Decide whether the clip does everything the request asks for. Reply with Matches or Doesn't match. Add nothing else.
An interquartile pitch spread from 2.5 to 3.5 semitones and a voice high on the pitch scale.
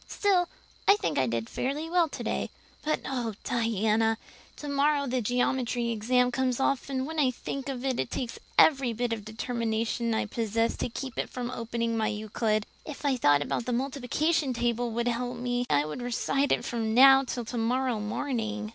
Matches